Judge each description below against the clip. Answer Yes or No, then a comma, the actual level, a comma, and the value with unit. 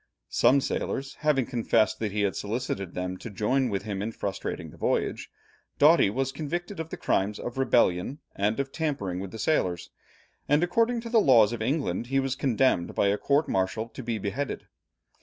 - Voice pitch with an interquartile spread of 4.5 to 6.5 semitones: Yes, wide, 5.5 semitones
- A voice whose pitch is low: Yes, low, 120 Hz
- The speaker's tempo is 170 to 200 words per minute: Yes, average, 190 wpm